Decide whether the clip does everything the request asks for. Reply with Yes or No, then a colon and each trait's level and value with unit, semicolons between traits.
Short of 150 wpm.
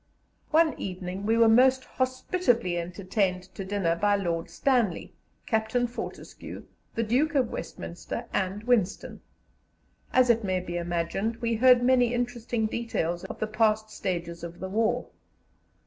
Yes: average, 140 wpm